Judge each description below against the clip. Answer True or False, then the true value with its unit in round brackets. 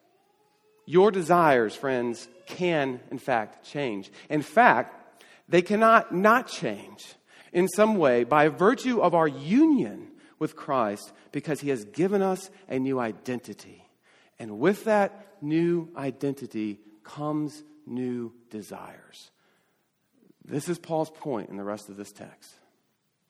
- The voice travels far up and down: True (8.2 semitones)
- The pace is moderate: False (125 wpm)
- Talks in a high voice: False (155 Hz)